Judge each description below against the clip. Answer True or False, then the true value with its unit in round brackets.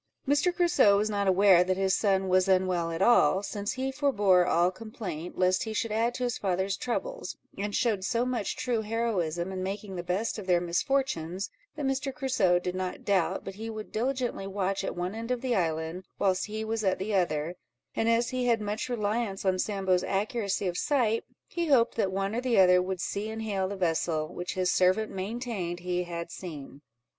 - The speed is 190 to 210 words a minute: True (205 wpm)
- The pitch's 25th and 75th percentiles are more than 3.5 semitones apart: True (4.0 semitones)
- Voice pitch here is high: True (195 Hz)